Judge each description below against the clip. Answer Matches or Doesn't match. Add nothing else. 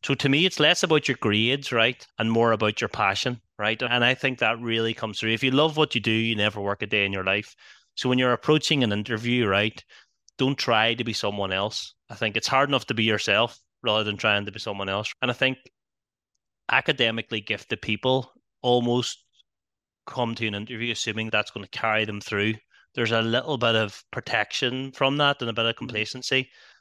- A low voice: Matches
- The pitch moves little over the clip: Doesn't match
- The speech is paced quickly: Matches